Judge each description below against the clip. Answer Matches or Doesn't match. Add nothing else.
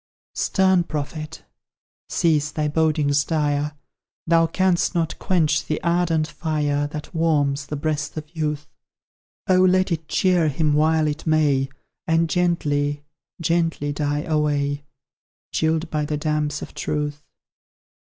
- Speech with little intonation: Matches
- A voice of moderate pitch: Matches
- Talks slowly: Matches